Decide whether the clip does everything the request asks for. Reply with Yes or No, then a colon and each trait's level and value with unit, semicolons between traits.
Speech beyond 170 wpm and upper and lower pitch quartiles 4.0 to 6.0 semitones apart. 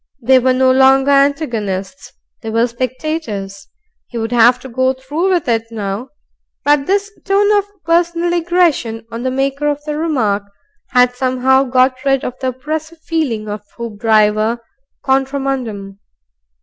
No: average, 150 wpm; average, 4.4 semitones